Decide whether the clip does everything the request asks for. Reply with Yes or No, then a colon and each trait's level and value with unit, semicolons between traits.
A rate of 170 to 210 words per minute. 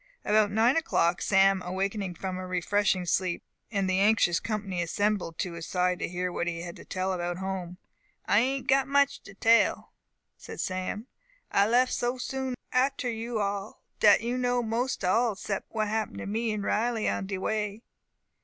Yes: average, 180 wpm